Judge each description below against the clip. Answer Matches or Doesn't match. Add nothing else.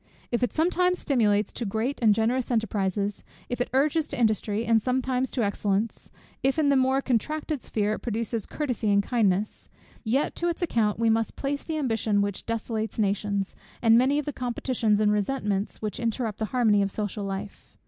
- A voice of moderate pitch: Doesn't match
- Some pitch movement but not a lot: Matches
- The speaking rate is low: Doesn't match